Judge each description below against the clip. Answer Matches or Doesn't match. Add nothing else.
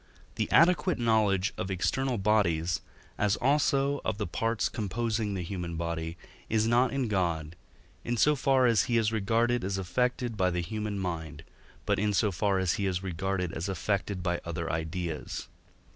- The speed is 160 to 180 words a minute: Matches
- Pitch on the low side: Matches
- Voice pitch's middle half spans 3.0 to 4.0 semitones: Doesn't match